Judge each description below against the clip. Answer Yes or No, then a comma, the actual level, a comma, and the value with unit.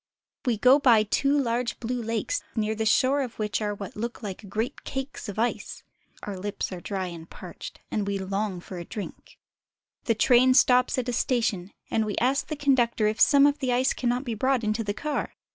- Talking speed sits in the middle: No, fast, 220 wpm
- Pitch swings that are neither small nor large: Yes, average, 3.6 semitones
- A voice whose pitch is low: No, high, 230 Hz